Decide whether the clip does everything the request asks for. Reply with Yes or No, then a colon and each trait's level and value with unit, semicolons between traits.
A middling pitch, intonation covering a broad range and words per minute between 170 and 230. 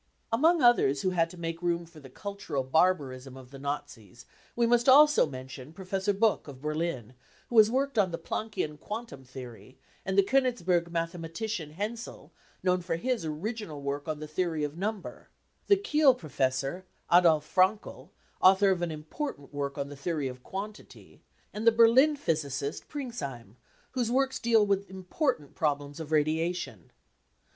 No: medium, 170 Hz; wide, 7.2 semitones; average, 160 wpm